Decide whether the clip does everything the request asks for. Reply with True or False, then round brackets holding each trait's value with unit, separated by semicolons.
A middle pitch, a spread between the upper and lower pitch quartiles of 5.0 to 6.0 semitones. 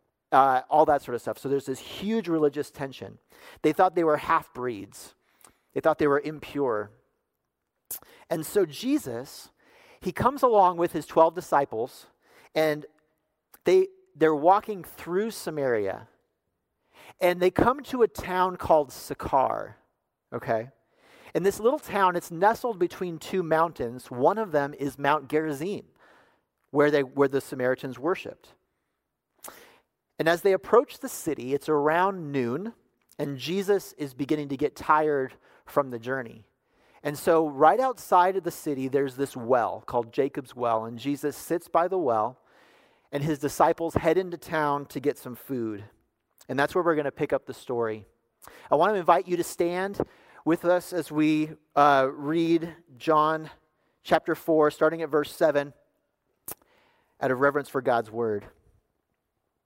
False (155 Hz; 4.2 semitones)